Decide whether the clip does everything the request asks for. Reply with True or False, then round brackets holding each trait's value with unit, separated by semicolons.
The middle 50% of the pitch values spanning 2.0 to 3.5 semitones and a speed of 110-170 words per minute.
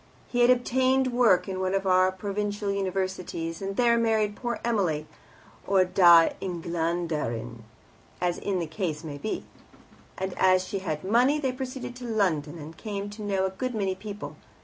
False (4.3 semitones; 165 wpm)